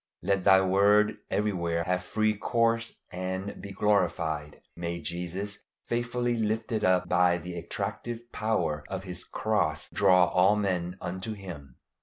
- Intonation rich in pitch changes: No, average, 3.3 semitones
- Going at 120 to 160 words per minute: Yes, slow, 135 wpm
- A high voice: No, very low, 95 Hz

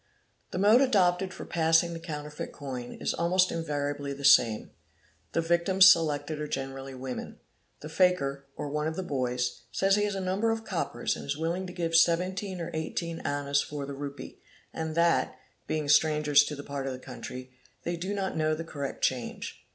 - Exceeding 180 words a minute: Yes, average, 190 wpm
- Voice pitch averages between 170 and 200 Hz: No, medium, 160 Hz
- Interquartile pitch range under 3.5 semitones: No, average, 4.1 semitones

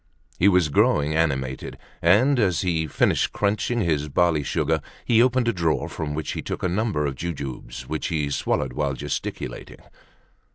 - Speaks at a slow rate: No, average, 170 wpm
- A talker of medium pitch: No, very low, 80 Hz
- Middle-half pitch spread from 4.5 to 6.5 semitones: Yes, wide, 5.5 semitones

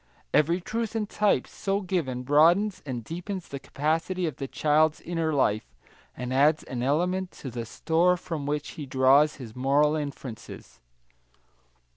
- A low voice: No, medium, 150 Hz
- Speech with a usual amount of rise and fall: Yes, average, 4.9 semitones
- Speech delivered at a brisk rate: No, average, 150 wpm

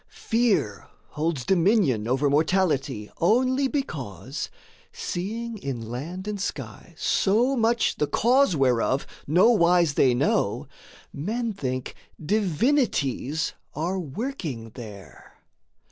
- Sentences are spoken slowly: Yes, slow, 100 wpm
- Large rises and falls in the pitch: Yes, wide, 8.9 semitones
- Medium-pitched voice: Yes, medium, 170 Hz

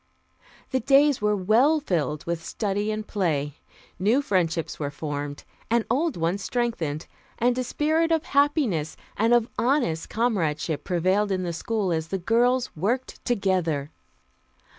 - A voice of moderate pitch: No, high, 205 Hz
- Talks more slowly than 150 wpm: Yes, average, 140 wpm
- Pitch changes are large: Yes, wide, 7.0 semitones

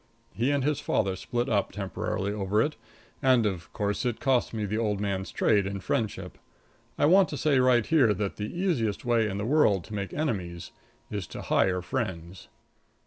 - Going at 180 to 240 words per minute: Yes, average, 190 wpm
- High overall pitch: No, low, 105 Hz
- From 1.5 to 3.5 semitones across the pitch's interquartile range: No, average, 4.6 semitones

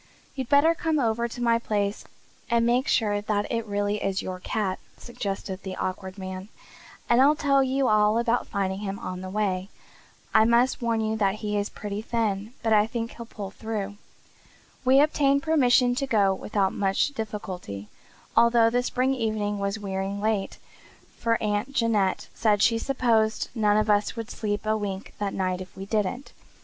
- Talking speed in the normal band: Yes, average, 180 wpm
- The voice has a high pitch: Yes, high, 215 Hz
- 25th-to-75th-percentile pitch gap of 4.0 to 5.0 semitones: No, average, 2.9 semitones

